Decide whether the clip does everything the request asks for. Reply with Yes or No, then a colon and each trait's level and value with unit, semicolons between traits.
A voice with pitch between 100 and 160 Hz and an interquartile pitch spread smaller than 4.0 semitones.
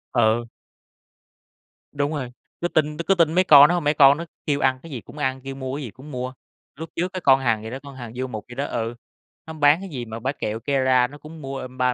Yes: low, 135 Hz; average, 3.2 semitones